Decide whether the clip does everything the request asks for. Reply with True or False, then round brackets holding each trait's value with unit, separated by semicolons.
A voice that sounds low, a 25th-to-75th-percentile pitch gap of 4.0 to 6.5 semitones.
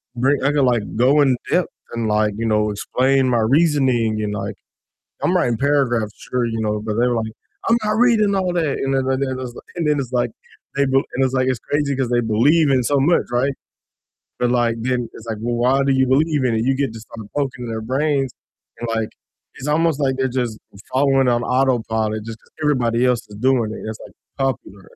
False (125 Hz; 3.3 semitones)